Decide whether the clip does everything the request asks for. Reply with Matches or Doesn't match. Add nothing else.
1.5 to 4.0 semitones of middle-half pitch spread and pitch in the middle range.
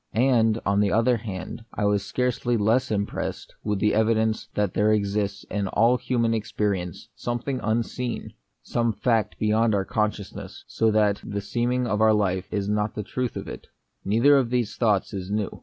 Doesn't match